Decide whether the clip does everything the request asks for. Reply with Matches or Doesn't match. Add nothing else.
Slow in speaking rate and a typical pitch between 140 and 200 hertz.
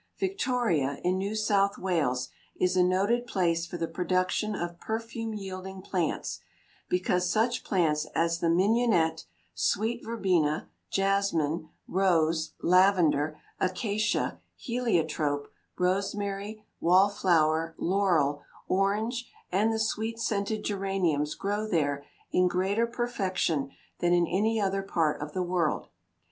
Matches